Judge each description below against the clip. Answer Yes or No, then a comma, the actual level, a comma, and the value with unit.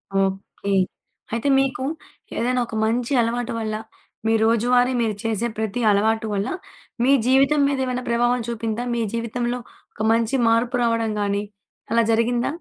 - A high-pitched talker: Yes, high, 230 Hz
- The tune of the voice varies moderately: No, narrow, 1.9 semitones